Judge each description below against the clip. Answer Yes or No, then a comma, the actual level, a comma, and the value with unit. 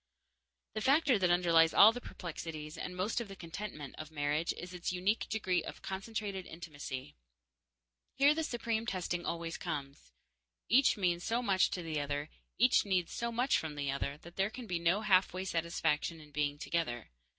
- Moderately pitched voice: Yes, medium, 175 Hz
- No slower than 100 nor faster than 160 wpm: No, average, 175 wpm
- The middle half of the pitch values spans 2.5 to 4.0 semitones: No, average, 5.0 semitones